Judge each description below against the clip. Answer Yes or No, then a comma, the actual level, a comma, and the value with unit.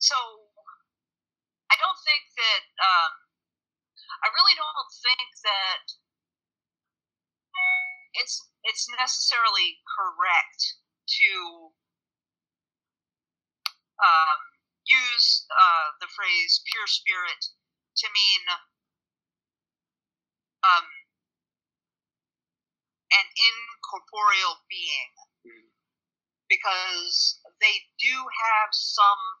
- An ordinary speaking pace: No, slow, 70 wpm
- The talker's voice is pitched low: No, very high, 255 Hz